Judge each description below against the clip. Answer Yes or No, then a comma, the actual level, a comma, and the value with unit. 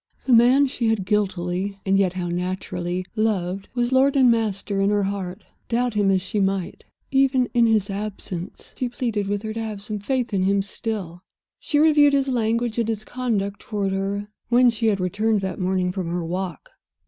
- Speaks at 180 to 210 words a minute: Yes, average, 195 wpm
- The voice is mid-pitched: No, high, 205 Hz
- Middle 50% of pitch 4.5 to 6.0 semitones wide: No, average, 3.5 semitones